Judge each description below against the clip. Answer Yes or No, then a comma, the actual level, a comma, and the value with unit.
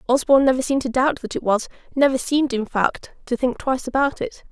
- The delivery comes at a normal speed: No, fast, 210 wpm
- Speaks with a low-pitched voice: No, very high, 260 Hz